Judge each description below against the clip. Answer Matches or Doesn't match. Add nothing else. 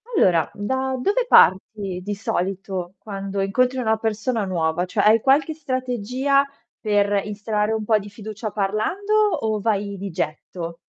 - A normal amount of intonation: Matches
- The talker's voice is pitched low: Doesn't match